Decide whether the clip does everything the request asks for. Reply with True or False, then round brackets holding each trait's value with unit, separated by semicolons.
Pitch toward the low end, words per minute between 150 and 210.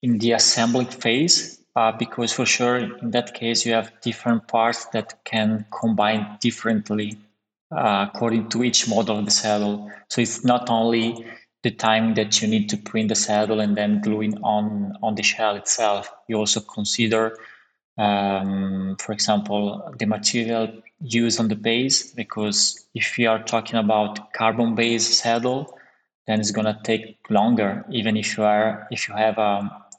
True (110 Hz; 165 wpm)